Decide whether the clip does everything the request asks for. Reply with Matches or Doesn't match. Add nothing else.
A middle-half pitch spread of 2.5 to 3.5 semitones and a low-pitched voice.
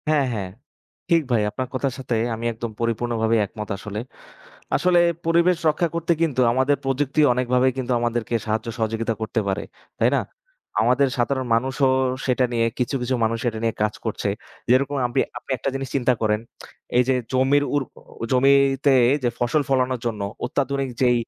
Matches